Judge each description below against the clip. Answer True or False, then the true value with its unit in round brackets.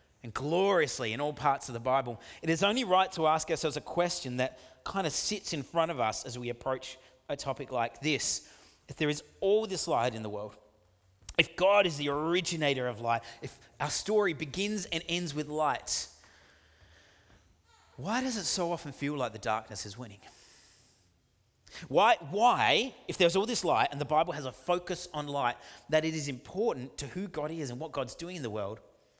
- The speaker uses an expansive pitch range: True (6.3 semitones)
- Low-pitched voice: False (145 Hz)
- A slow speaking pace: False (200 wpm)